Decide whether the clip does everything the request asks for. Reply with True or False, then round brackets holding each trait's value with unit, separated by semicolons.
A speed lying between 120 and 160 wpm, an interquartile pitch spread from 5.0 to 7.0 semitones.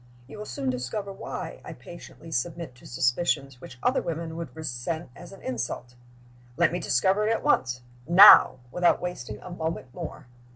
False (170 wpm; 5.6 semitones)